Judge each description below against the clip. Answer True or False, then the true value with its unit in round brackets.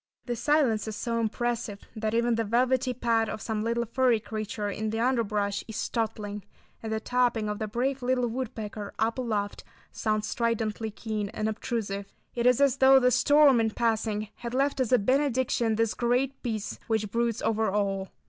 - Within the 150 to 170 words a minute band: False (180 wpm)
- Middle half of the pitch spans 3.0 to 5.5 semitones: False (2.5 semitones)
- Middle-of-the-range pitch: False (225 Hz)